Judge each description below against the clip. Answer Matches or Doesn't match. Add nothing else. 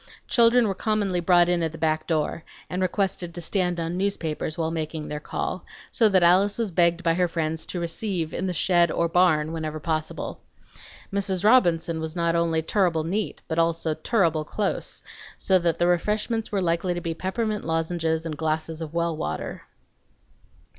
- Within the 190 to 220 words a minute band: Doesn't match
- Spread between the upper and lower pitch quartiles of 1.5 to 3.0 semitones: Matches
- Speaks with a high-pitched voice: Doesn't match